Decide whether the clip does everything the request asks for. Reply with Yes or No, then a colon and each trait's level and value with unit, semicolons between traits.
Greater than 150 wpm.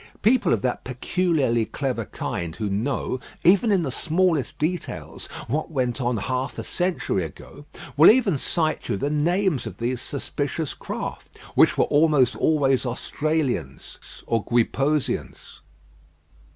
No: slow, 135 wpm